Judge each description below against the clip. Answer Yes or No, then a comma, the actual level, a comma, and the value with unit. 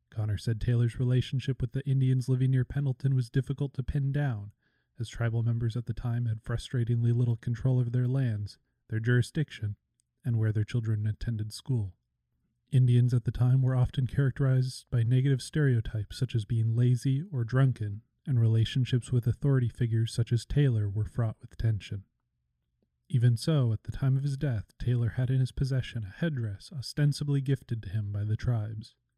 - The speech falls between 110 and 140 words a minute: No, average, 175 wpm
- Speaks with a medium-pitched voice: No, low, 120 Hz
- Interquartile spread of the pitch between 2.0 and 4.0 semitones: Yes, average, 3.0 semitones